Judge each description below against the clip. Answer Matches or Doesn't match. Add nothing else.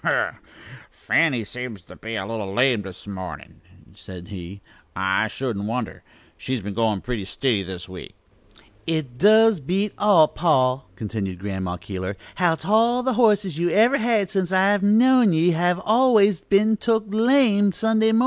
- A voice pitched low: Doesn't match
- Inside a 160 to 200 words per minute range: Matches